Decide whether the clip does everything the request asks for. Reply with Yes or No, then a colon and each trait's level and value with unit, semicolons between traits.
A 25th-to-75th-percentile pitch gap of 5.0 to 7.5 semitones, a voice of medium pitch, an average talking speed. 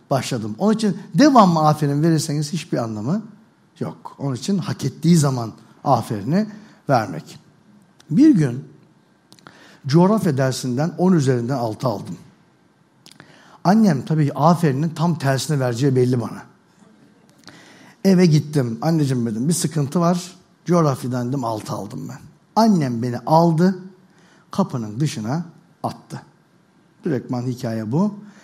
Yes: average, 5.3 semitones; medium, 155 Hz; average, 115 wpm